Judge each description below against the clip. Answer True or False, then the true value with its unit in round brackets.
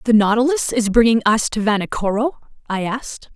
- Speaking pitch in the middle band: False (225 Hz)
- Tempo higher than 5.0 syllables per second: True (5.6 syllables/s)